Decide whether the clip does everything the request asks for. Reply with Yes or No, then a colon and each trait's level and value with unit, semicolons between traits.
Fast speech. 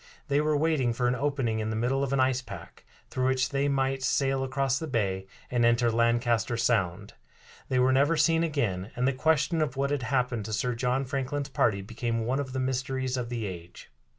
Yes: fast, 210 wpm